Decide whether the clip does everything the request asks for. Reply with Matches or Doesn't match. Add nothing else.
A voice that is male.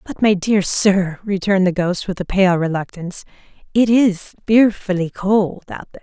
Doesn't match